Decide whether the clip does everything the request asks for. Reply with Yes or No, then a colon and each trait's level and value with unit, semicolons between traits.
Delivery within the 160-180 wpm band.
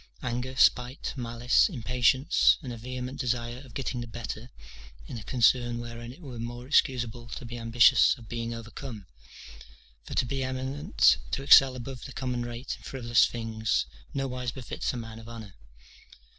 Yes: average, 165 wpm